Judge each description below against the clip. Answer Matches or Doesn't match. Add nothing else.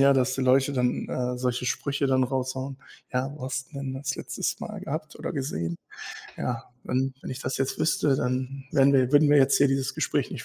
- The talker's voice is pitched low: Matches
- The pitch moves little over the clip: Matches